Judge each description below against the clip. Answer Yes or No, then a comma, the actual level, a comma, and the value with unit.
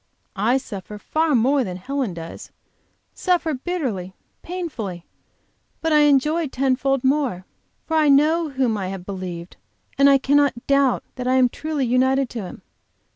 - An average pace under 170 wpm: Yes, average, 155 wpm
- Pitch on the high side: Yes, very high, 265 Hz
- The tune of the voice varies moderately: No, wide, 5.8 semitones